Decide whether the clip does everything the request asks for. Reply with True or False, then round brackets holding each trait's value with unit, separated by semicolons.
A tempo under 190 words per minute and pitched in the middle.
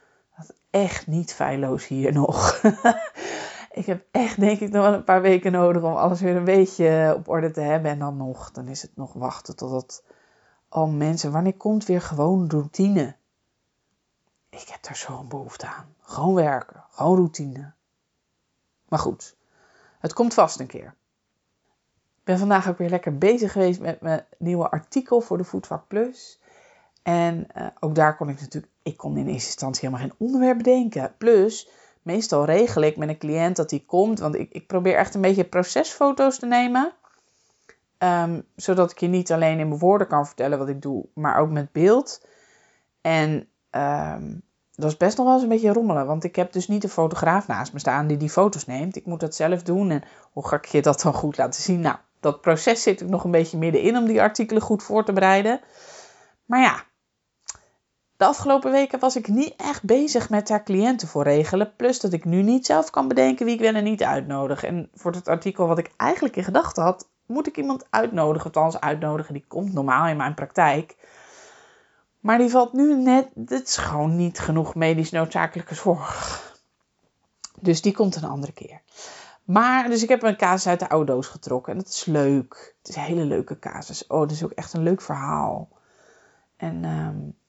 False (195 wpm; 175 Hz)